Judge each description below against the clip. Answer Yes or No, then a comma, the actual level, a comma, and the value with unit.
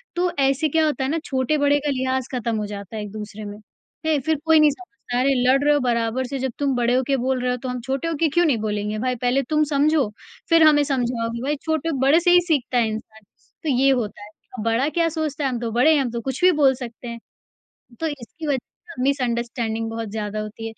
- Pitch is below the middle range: No, very high, 260 Hz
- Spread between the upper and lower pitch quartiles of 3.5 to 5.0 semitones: Yes, average, 4.1 semitones